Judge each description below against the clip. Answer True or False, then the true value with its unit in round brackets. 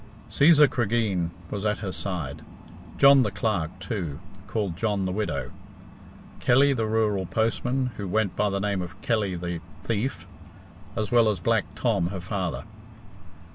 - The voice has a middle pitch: False (105 Hz)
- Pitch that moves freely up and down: False (3.7 semitones)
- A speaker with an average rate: True (150 wpm)